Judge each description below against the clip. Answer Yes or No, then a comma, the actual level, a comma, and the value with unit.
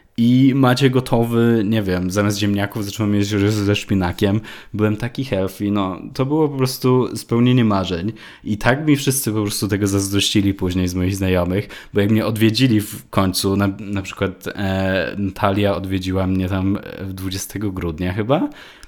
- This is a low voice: Yes, low, 105 Hz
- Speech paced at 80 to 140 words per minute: No, fast, 160 wpm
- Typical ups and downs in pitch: Yes, average, 3.1 semitones